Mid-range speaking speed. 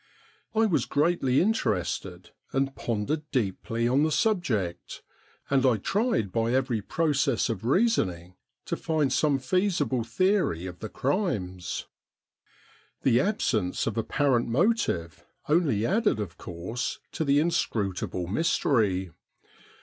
No: slow, 120 wpm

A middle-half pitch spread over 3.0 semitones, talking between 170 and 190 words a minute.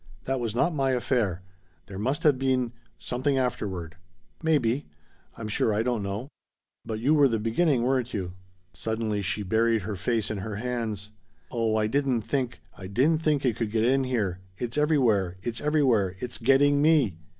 Yes: average, 4.1 semitones; average, 175 wpm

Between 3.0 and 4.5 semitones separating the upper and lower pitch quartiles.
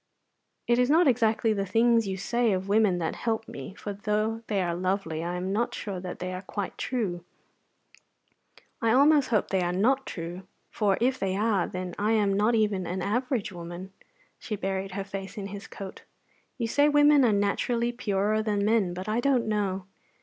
Yes: average, 3.4 semitones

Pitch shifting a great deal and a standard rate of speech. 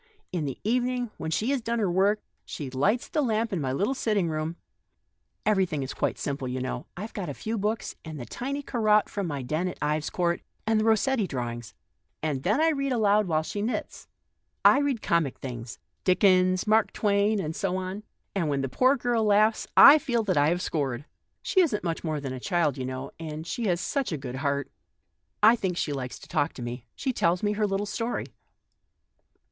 No: wide, 6.9 semitones; fast, 215 wpm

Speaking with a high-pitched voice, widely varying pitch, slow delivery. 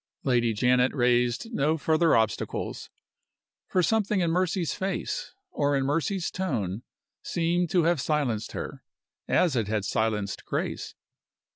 No: medium, 145 Hz; wide, 6.6 semitones; slow, 130 wpm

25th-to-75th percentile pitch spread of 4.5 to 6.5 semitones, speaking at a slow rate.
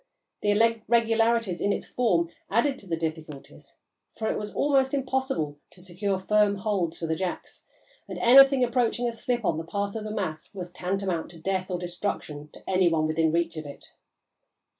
No: wide, 5.4 semitones; average, 180 wpm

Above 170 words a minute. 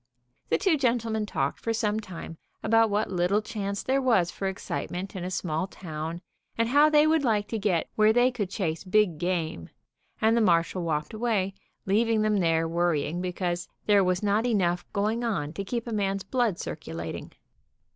Yes: average, 180 wpm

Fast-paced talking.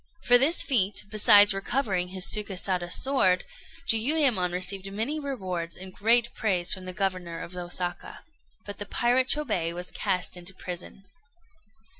No: average, 140 wpm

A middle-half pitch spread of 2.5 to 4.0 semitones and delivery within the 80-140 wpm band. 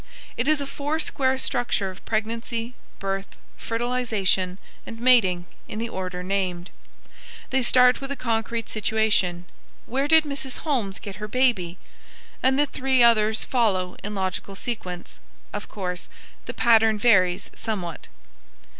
No: average, 4.7 semitones; slow, 135 wpm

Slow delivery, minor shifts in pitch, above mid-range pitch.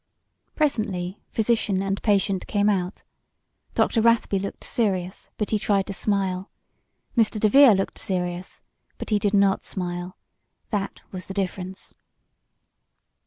Yes: slow, 125 wpm; narrow, 2.3 semitones; high, 195 Hz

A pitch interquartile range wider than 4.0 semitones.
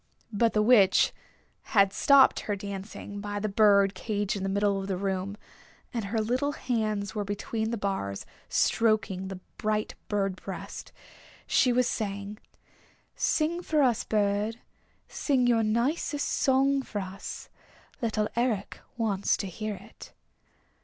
No: average, 2.8 semitones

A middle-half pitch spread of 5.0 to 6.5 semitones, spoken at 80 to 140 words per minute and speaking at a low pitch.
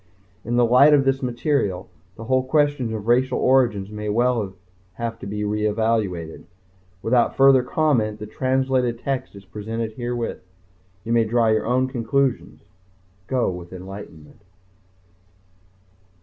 No: average, 3.6 semitones; slow, 135 wpm; low, 115 Hz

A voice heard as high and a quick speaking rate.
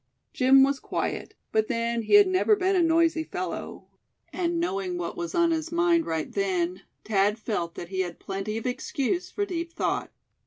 No: very high, 265 Hz; average, 185 wpm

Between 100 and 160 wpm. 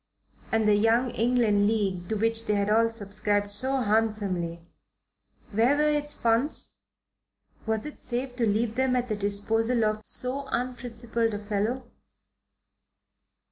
Yes: average, 140 wpm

